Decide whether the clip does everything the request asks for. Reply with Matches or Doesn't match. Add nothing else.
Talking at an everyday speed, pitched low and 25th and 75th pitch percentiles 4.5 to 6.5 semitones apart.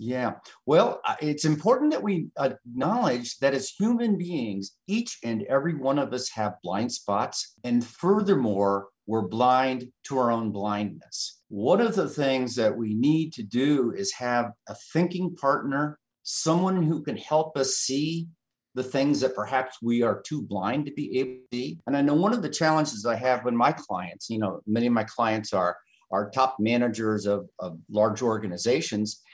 Matches